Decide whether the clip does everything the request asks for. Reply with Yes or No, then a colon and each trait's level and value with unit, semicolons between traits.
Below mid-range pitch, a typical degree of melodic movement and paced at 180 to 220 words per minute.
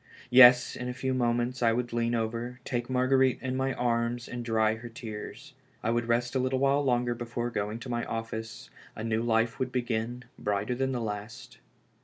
No: low, 120 Hz; narrow, 1.7 semitones; average, 195 wpm